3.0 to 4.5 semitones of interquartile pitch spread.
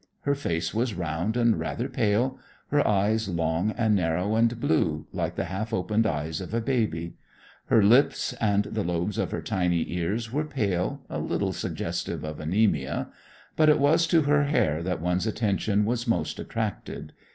No: average, 5.1 semitones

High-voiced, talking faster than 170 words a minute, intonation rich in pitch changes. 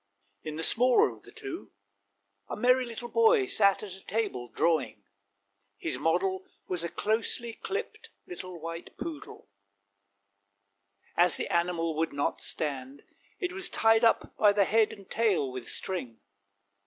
No: high, 195 Hz; average, 145 wpm; wide, 6.5 semitones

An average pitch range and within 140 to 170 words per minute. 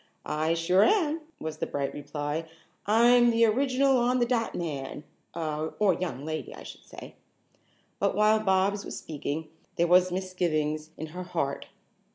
No: wide, 6.4 semitones; average, 155 wpm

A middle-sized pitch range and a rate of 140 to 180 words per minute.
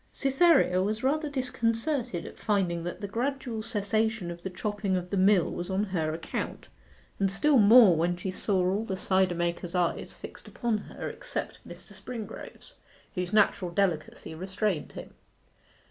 Yes: average, 3.9 semitones; average, 160 wpm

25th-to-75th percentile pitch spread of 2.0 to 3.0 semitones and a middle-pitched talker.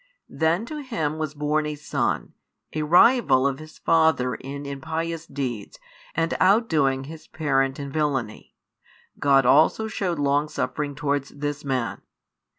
Yes: average, 2.7 semitones; medium, 150 Hz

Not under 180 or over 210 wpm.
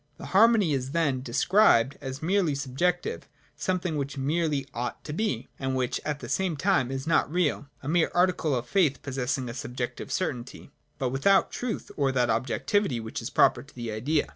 Yes: average, 190 wpm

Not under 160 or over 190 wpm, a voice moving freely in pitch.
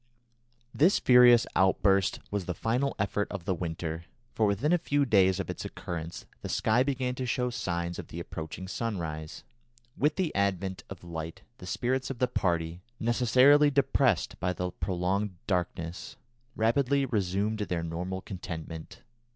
No: average, 150 wpm; wide, 6.1 semitones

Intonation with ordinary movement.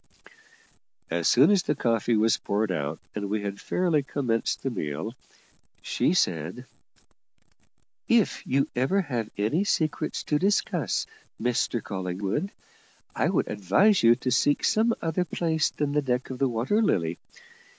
No: wide, 7.3 semitones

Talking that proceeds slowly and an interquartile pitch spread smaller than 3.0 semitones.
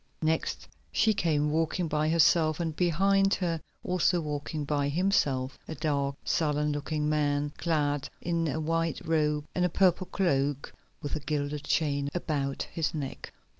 No: average, 150 wpm; narrow, 2.4 semitones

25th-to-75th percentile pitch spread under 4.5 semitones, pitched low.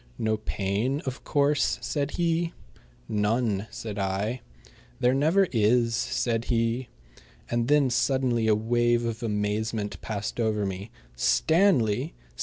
Yes: average, 3.6 semitones; low, 115 Hz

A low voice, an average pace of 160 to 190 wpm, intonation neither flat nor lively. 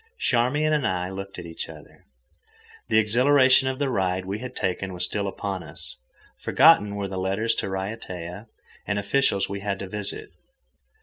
Yes: low, 100 Hz; average, 170 wpm; average, 3.9 semitones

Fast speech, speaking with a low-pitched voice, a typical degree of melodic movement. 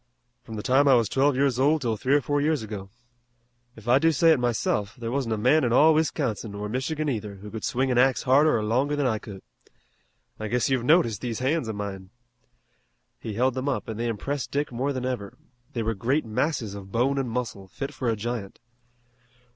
Yes: fast, 220 wpm; low, 125 Hz; average, 4.0 semitones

